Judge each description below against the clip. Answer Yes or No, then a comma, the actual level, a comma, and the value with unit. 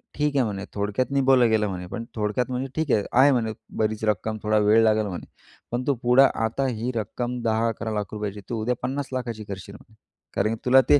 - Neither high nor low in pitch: No, low, 115 Hz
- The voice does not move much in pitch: No, average, 3.0 semitones